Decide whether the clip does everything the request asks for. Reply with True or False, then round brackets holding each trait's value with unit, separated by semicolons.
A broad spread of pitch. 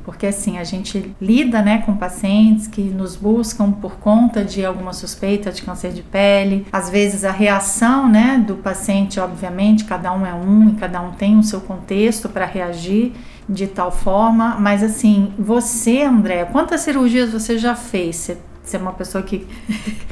False (2.5 semitones)